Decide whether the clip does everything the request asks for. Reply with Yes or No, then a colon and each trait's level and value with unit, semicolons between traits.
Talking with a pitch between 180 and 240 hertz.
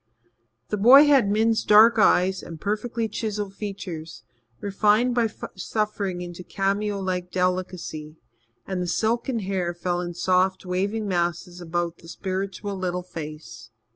Yes: high, 190 Hz